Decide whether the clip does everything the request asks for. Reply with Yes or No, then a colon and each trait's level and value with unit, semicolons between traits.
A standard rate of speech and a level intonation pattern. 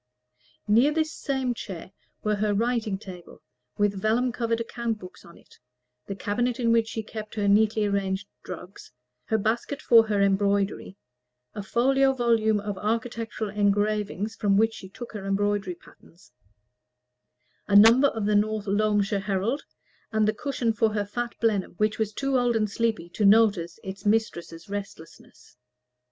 Yes: average, 155 wpm; narrow, 2.3 semitones